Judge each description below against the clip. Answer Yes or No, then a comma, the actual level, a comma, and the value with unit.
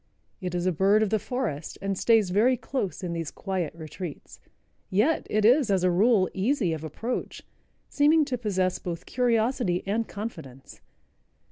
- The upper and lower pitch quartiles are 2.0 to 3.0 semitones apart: No, average, 4.7 semitones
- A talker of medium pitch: No, high, 195 Hz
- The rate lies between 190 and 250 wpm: No, average, 160 wpm